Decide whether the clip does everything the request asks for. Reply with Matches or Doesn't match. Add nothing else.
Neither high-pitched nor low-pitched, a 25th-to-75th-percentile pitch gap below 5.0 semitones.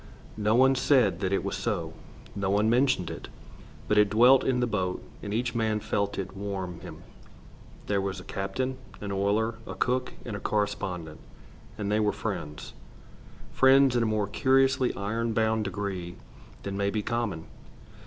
Doesn't match